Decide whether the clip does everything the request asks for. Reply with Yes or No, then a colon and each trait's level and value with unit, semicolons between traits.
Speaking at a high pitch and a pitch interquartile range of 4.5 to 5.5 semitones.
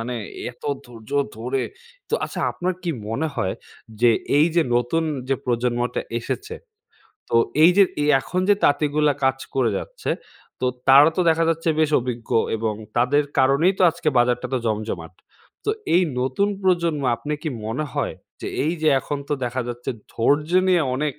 No: medium, 140 Hz; average, 5.2 semitones